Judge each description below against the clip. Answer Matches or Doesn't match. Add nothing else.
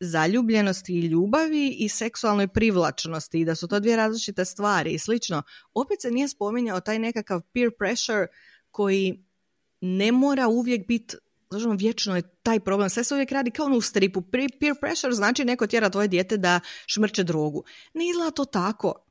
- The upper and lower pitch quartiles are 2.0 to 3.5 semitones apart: Doesn't match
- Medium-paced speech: Doesn't match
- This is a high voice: Matches